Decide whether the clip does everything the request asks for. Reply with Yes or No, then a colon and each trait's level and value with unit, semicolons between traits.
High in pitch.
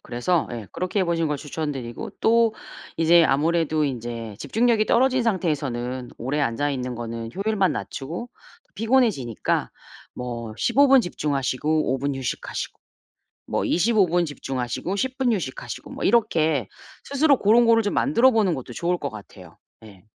No: medium, 160 Hz